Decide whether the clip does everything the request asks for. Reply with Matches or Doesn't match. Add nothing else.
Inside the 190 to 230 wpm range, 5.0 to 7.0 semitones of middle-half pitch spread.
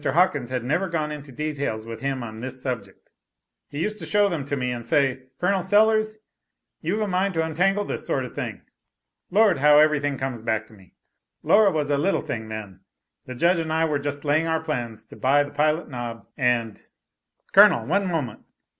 Matches